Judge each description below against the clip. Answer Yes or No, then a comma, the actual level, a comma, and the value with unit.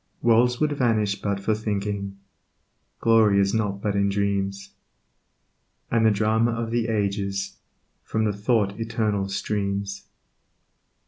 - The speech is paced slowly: Yes, slow, 125 wpm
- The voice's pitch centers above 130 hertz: No, low, 105 Hz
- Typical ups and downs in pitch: No, narrow, 2.2 semitones